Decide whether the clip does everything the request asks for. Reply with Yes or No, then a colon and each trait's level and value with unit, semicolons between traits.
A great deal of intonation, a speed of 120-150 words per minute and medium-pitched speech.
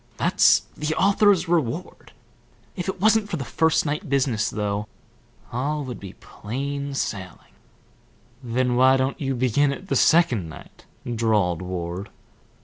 No: wide, 6.2 semitones; average, 140 wpm; low, 130 Hz